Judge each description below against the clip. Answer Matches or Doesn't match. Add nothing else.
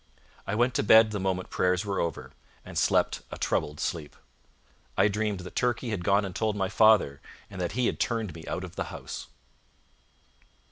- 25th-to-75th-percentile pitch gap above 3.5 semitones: Doesn't match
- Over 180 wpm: Matches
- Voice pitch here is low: Matches